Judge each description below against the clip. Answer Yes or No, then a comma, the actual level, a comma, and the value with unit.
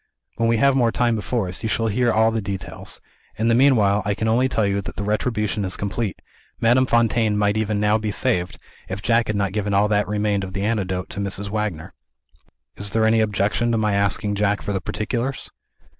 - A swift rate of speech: Yes, fast, 215 wpm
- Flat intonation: Yes, narrow, 2.2 semitones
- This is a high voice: No, low, 105 Hz